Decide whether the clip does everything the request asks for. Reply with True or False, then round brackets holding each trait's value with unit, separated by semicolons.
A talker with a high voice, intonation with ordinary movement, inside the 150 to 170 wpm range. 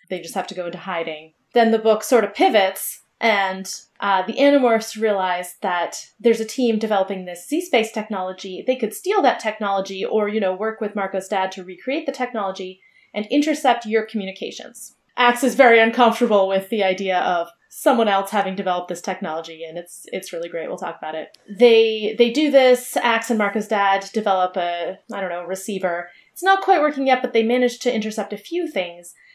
False (210 Hz; 4.3 semitones; 195 wpm)